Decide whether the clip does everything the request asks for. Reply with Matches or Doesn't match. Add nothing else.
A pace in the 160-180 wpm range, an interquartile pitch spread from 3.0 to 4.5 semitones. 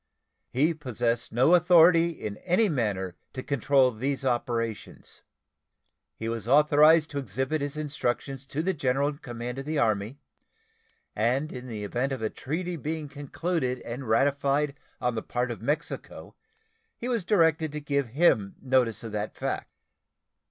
Doesn't match